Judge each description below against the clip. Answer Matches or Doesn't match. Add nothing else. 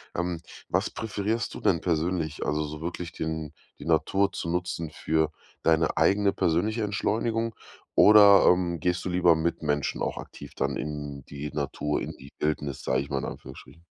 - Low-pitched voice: Matches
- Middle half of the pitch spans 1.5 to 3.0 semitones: Doesn't match